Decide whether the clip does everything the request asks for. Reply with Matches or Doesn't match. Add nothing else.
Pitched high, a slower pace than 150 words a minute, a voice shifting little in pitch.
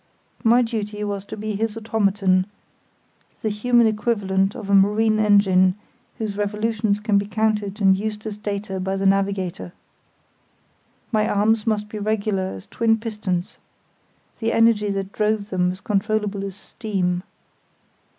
Matches